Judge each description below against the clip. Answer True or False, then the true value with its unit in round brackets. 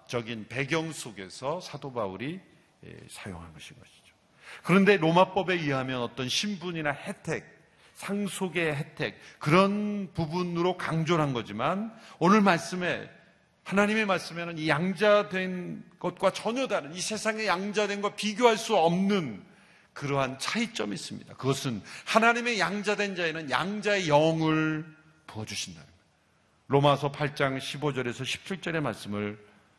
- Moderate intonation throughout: False (5.9 semitones)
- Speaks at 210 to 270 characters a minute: False (290 characters per minute)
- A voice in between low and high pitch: True (170 Hz)